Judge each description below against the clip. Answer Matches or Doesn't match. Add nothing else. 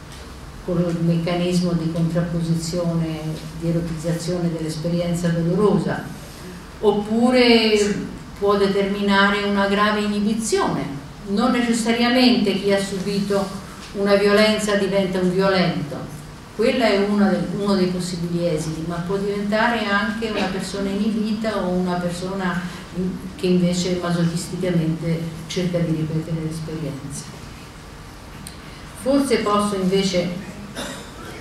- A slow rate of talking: Matches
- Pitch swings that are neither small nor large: Matches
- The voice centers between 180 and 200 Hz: Matches